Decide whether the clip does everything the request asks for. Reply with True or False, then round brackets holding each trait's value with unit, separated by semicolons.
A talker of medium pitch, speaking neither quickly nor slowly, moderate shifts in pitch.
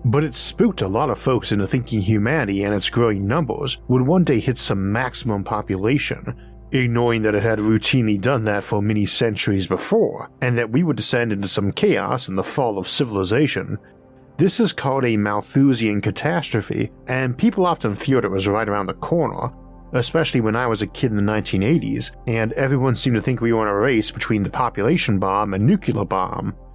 False (115 Hz; 195 wpm; 4.2 semitones)